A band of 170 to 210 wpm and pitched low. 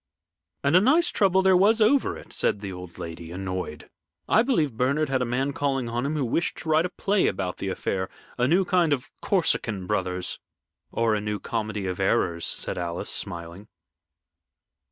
Yes: average, 185 wpm; low, 120 Hz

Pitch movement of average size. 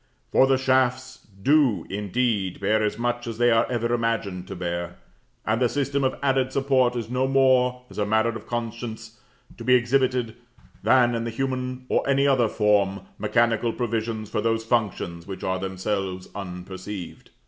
Yes: average, 3.5 semitones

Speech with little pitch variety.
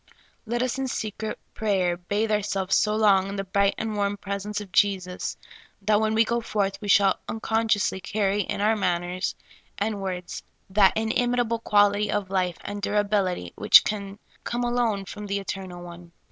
Yes: narrow, 2.0 semitones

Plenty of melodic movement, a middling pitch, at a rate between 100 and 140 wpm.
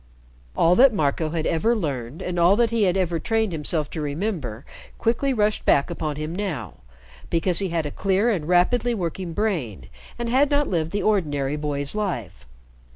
No: wide, 5.8 semitones; medium, 175 Hz; average, 180 wpm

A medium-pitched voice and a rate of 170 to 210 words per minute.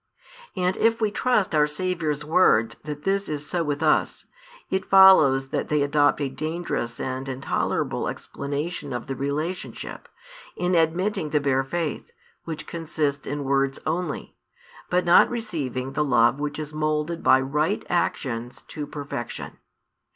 No: medium, 150 Hz; average, 145 wpm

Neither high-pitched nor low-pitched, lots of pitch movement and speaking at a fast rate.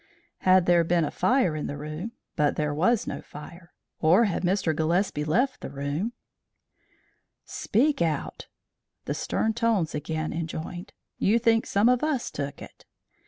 No: medium, 175 Hz; wide, 6.3 semitones; average, 160 wpm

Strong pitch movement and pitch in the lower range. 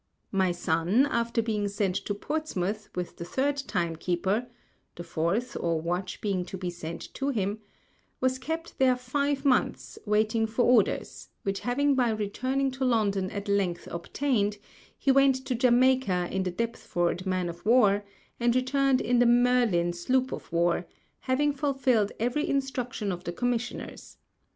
No: wide, 5.7 semitones; high, 225 Hz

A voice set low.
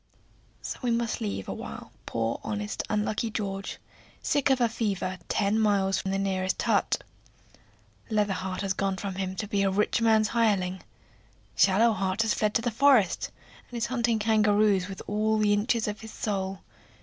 No: high, 210 Hz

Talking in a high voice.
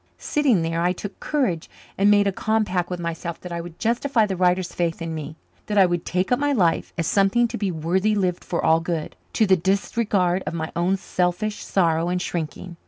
No: medium, 180 Hz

